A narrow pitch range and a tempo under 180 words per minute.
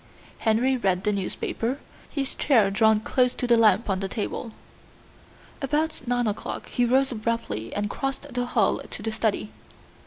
No: average, 3.5 semitones; average, 160 wpm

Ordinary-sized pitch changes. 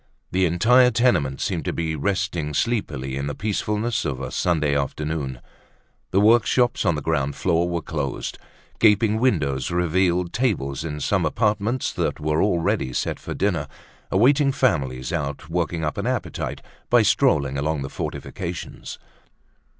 No: wide, 6.4 semitones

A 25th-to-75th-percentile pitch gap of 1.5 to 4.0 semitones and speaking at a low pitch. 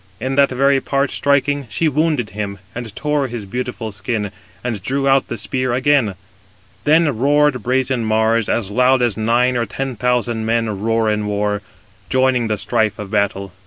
Yes: average, 3.7 semitones; low, 120 Hz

